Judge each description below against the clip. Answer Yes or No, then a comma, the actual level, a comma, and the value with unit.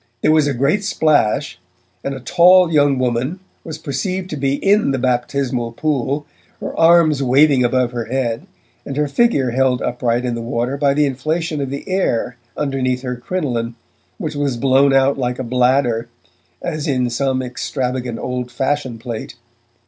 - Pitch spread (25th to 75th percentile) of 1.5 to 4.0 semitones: Yes, average, 3.1 semitones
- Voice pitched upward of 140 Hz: No, low, 135 Hz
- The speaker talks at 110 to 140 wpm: No, average, 165 wpm